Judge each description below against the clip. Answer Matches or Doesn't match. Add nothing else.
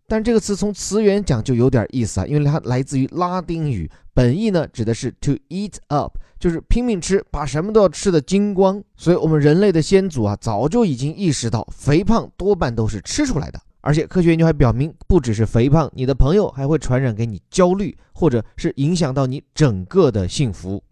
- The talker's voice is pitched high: Doesn't match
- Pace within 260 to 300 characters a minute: Doesn't match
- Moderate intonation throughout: Doesn't match